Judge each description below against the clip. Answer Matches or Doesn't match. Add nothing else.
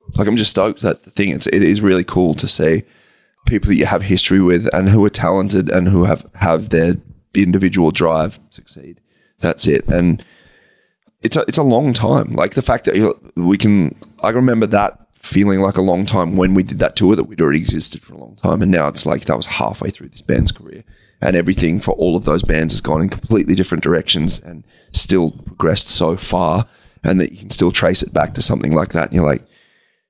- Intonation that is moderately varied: Doesn't match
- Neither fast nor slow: Doesn't match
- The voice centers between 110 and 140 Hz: Doesn't match